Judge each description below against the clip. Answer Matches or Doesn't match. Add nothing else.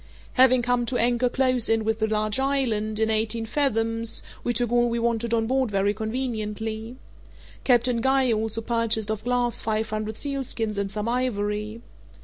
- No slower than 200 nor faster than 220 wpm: Doesn't match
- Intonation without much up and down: Matches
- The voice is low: Doesn't match